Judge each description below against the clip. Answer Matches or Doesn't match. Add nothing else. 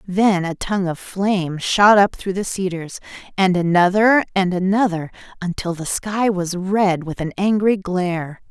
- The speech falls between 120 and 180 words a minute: Matches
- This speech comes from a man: Doesn't match